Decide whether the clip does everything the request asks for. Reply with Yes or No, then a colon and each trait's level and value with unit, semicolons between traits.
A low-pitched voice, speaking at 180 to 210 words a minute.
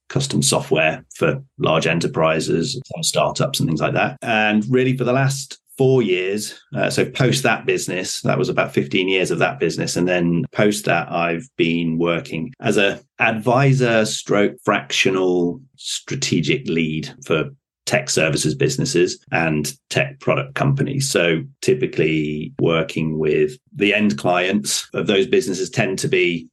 No: low, 100 Hz; average, 145 wpm